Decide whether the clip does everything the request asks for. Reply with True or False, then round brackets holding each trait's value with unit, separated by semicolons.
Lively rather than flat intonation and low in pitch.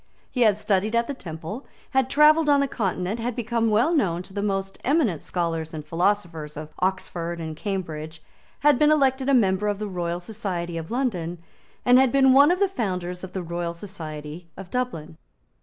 False (6.5 semitones; 195 Hz)